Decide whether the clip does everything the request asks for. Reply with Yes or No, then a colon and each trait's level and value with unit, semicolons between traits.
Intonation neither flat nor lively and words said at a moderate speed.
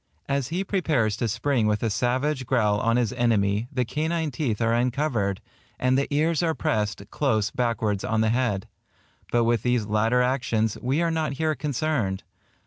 Yes: average, 4.6 semitones; average, 175 wpm